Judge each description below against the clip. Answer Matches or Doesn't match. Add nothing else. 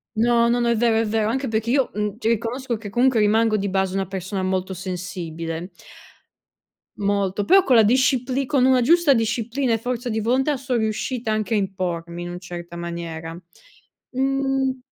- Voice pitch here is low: Doesn't match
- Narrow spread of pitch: Doesn't match